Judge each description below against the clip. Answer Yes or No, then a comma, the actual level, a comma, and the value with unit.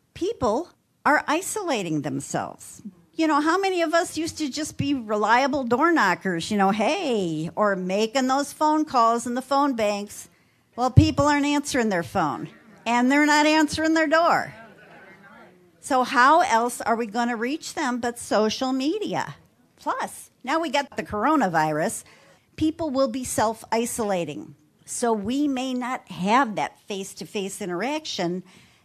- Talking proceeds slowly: No, average, 155 wpm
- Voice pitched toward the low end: No, very high, 250 Hz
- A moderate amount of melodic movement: No, wide, 6.1 semitones